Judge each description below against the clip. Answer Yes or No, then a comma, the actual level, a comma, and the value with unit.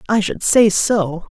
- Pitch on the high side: Yes, high, 200 Hz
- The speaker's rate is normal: Yes, average, 175 wpm